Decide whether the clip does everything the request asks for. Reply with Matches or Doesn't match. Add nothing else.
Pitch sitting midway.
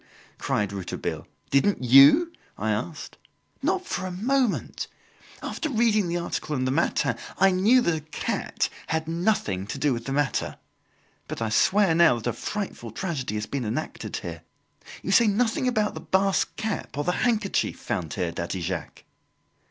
Matches